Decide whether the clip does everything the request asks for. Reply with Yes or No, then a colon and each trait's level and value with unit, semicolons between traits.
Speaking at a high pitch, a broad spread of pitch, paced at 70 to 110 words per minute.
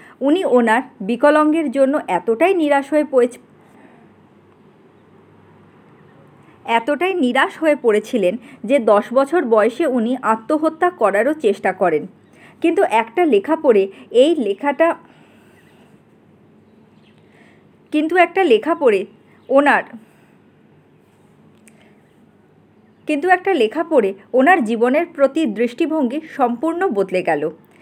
Yes: very high, 280 Hz; wide, 6.2 semitones; average, 95 wpm